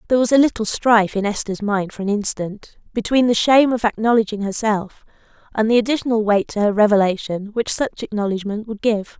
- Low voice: No, high, 215 Hz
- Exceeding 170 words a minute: Yes, average, 190 wpm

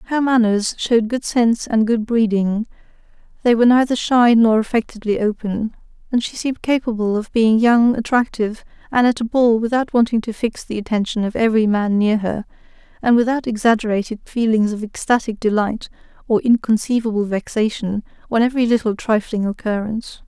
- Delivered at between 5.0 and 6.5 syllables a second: Yes, 5.5 syllables/s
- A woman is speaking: Yes, female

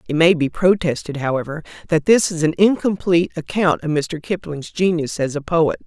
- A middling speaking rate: Yes, average, 185 wpm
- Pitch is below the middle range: No, medium, 165 Hz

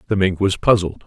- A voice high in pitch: No, very low, 95 Hz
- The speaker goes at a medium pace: No, fast, 225 wpm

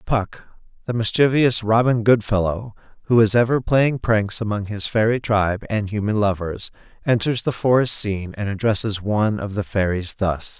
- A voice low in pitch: Yes, low, 110 Hz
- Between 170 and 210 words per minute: No, average, 160 wpm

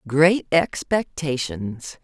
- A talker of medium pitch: Yes, medium, 150 Hz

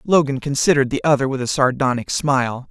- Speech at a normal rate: Yes, average, 175 wpm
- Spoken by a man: Yes, male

